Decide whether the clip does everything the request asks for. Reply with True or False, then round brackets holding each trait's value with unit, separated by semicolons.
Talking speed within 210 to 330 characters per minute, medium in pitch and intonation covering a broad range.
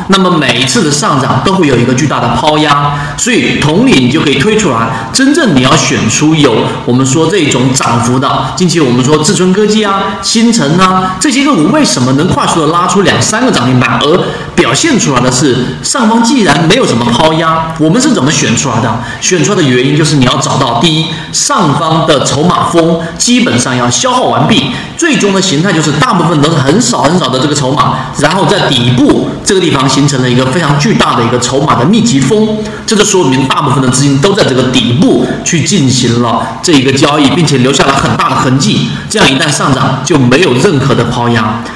True (325 characters per minute; 150 Hz; 6.0 semitones)